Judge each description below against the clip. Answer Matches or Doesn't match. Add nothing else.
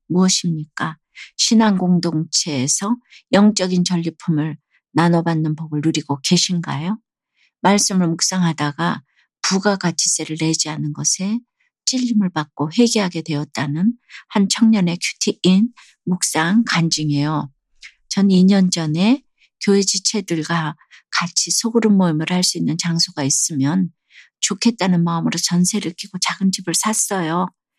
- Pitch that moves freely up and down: Doesn't match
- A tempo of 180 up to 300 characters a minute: Matches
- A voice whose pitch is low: Doesn't match